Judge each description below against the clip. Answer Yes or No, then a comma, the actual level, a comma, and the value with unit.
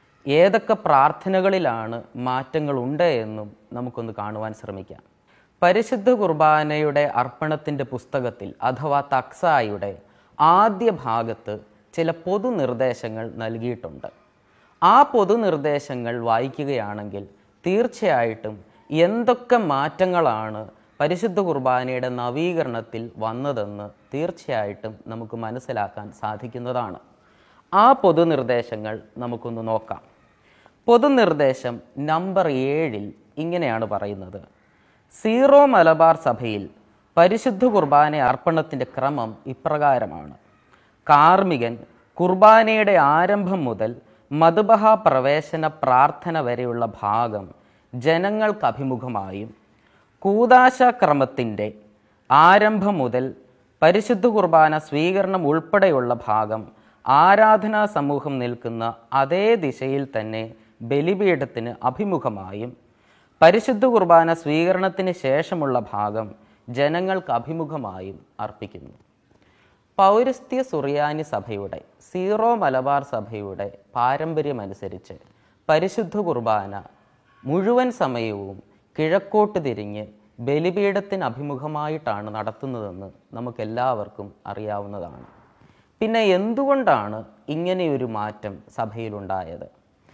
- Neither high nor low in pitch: No, low, 130 Hz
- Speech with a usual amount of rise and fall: No, wide, 7.7 semitones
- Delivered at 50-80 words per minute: Yes, average, 70 wpm